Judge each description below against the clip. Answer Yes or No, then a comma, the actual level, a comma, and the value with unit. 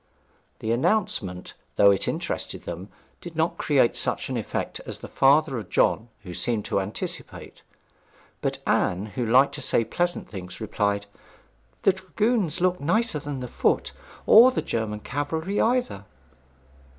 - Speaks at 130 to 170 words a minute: Yes, average, 150 wpm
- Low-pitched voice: Yes, low, 130 Hz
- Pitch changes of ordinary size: No, wide, 9.0 semitones